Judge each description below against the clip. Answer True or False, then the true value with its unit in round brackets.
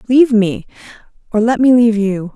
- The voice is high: True (225 Hz)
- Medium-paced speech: True (180 wpm)